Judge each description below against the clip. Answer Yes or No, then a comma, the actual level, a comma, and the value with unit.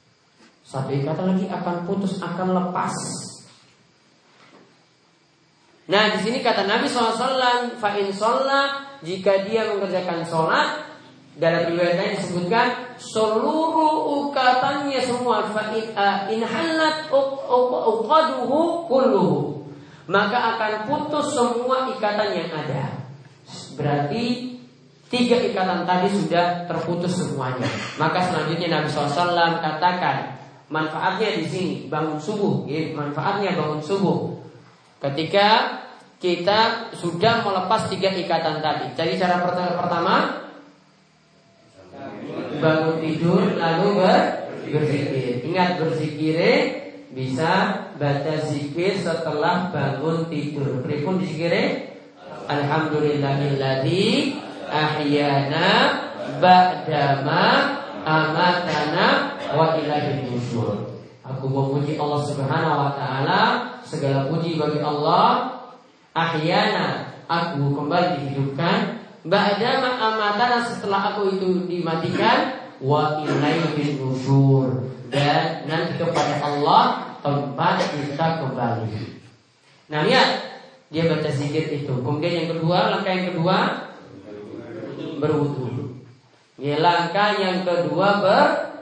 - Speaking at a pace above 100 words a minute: No, slow, 90 wpm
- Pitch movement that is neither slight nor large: No, wide, 6.1 semitones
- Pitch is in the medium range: Yes, medium, 175 Hz